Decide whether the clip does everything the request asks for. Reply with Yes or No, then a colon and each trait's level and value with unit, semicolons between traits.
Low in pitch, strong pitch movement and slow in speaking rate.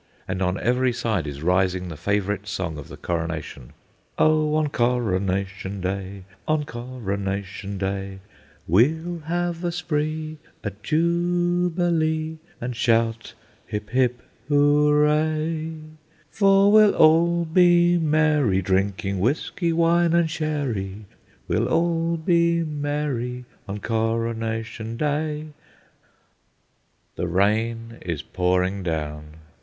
Yes: low, 125 Hz; wide, 8.4 semitones; slow, 105 wpm